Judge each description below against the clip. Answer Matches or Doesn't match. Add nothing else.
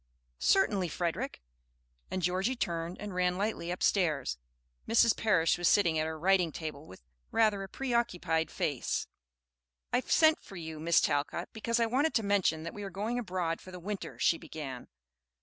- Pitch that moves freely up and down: Doesn't match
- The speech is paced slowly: Doesn't match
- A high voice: Doesn't match